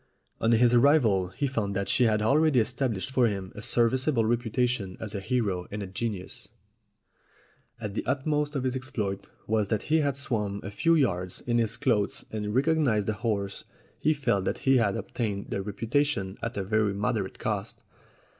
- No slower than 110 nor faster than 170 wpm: No, average, 185 wpm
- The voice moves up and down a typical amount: Yes, average, 4.4 semitones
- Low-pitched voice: Yes, low, 110 Hz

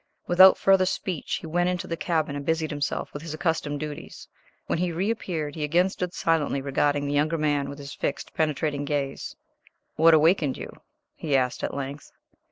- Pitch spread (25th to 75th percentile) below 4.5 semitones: Yes, average, 2.9 semitones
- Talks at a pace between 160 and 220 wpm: Yes, average, 185 wpm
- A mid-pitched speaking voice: Yes, medium, 155 Hz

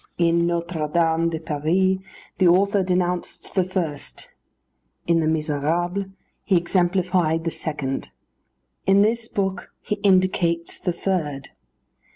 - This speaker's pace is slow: Yes, slow, 120 wpm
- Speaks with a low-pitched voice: No, medium, 175 Hz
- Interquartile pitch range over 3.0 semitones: No, narrow, 2.6 semitones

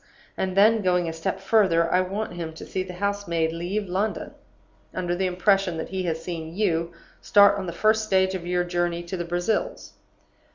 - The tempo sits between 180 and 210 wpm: Yes, average, 200 wpm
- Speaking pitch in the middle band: Yes, medium, 180 Hz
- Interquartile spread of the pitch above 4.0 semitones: No, average, 2.8 semitones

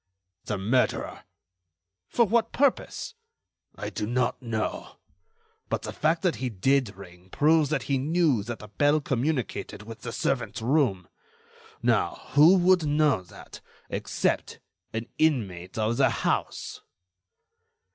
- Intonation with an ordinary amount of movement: No, wide, 6.1 semitones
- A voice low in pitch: Yes, low, 130 Hz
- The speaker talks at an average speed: No, slow, 130 wpm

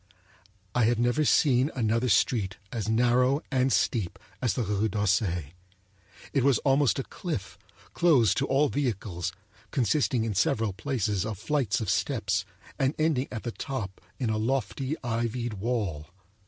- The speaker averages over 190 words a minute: No, average, 150 wpm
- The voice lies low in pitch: Yes, low, 120 Hz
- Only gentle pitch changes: No, average, 4.3 semitones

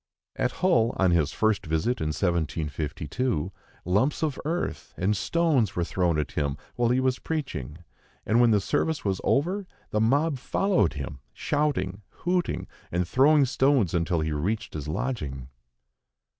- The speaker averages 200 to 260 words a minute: No, average, 150 wpm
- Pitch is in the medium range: No, low, 105 Hz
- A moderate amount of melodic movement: No, wide, 9.0 semitones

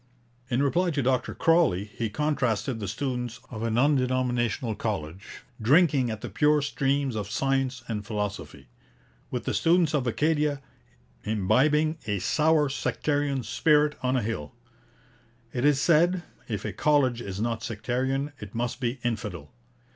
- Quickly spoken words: No, average, 145 wpm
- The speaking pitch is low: Yes, low, 125 Hz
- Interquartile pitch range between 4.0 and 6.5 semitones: Yes, average, 4.8 semitones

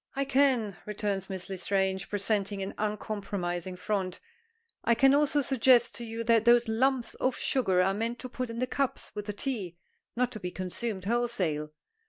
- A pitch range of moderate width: Yes, average, 4.1 semitones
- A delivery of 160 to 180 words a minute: Yes, average, 175 wpm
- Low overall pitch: No, high, 215 Hz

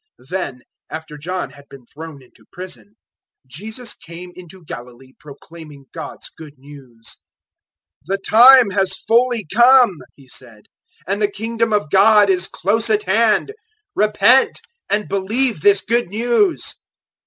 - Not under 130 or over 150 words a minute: Yes, average, 140 wpm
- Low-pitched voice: No, high, 190 Hz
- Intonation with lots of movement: Yes, wide, 6.7 semitones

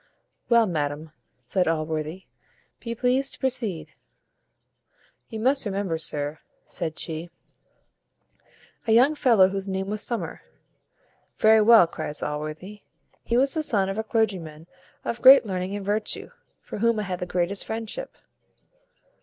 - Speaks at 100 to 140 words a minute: Yes, slow, 135 wpm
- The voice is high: Yes, high, 200 Hz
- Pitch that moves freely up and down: Yes, wide, 5.9 semitones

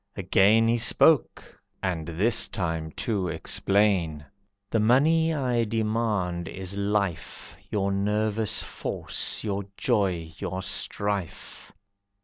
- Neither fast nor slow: No, slow, 105 wpm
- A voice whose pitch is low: Yes, low, 100 Hz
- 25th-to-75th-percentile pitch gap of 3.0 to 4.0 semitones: Yes, average, 3.5 semitones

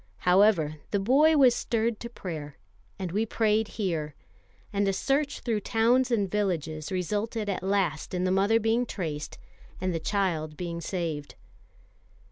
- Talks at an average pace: Yes, average, 150 wpm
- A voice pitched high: Yes, high, 195 Hz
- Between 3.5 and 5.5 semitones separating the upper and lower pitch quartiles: Yes, average, 4.9 semitones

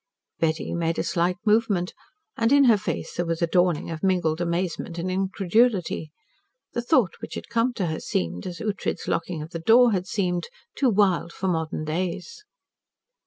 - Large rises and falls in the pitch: No, average, 4.2 semitones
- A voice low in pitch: No, medium, 180 Hz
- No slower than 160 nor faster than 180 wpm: Yes, average, 175 wpm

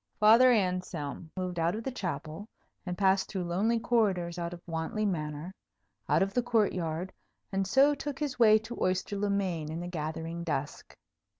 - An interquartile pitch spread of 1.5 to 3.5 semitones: No, average, 4.2 semitones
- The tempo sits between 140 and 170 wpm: No, average, 180 wpm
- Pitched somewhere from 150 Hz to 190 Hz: Yes, medium, 185 Hz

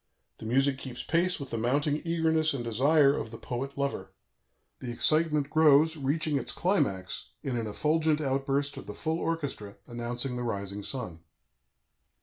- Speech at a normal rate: Yes, average, 155 wpm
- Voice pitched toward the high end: No, medium, 140 Hz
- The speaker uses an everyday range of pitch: Yes, average, 4.5 semitones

